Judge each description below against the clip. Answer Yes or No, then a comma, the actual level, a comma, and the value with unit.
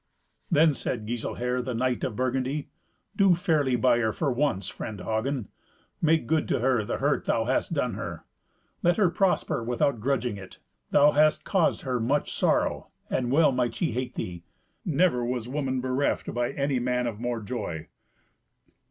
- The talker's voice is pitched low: Yes, low, 125 Hz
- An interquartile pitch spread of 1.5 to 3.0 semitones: No, average, 3.6 semitones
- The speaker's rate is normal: Yes, average, 170 wpm